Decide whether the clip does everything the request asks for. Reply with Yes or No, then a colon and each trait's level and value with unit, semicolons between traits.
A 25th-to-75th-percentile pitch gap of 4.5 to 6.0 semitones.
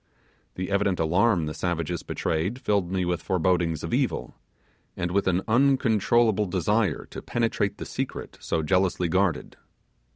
No: average, 3.2 semitones